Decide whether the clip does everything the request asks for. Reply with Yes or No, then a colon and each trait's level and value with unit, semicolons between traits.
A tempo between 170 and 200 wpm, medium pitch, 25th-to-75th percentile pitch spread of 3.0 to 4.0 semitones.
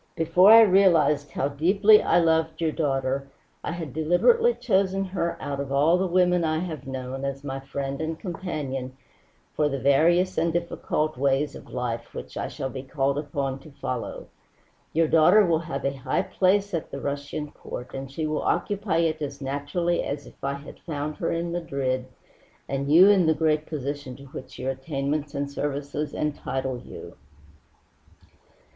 Yes: average, 175 wpm; medium, 150 Hz; average, 3.7 semitones